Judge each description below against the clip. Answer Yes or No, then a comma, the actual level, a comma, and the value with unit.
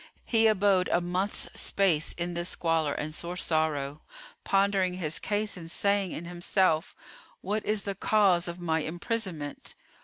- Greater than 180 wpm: No, average, 150 wpm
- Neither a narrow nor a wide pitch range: Yes, average, 3.5 semitones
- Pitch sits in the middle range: Yes, medium, 180 Hz